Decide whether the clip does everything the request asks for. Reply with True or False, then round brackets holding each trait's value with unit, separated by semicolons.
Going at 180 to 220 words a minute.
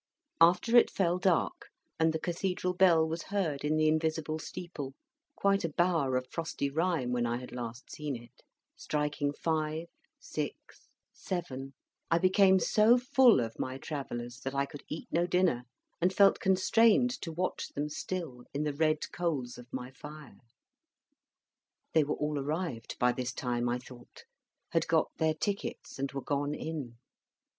False (160 wpm)